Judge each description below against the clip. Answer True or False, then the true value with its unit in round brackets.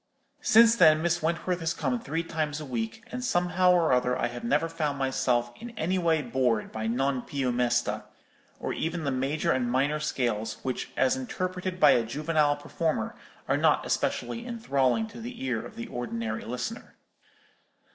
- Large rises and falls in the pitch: True (6.0 semitones)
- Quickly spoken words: False (175 wpm)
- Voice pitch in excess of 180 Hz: False (150 Hz)